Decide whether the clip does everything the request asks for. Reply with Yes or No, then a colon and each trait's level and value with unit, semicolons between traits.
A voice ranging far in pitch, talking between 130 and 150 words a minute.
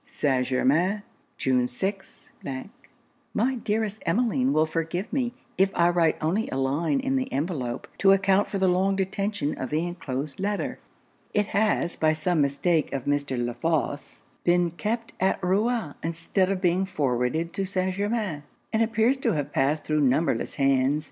No: wide, 5.8 semitones; average, 160 wpm